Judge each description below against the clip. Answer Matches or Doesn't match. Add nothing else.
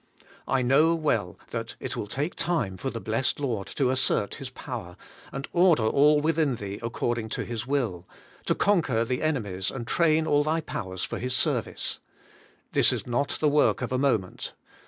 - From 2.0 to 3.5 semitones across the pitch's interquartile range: Doesn't match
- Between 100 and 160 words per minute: Doesn't match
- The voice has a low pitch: Matches